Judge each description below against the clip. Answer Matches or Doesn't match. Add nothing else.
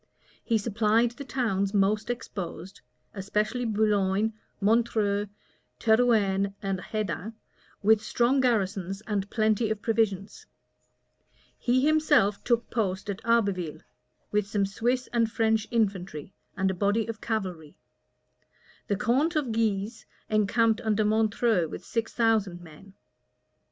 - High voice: Matches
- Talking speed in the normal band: Doesn't match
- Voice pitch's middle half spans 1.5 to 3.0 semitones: Matches